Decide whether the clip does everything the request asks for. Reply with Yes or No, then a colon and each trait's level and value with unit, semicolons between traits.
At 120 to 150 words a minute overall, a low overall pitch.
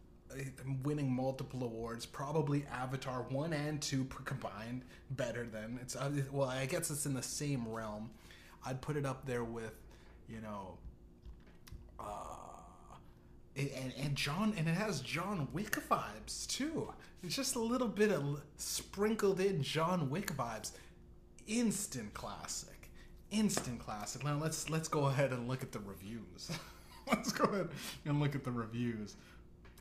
Yes: average, 145 wpm; low, 130 Hz